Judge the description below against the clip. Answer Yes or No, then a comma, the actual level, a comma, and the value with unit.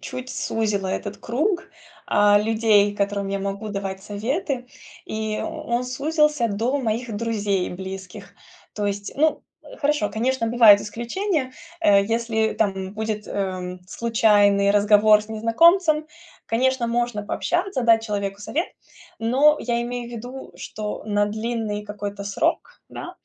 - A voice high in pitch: Yes, high, 220 Hz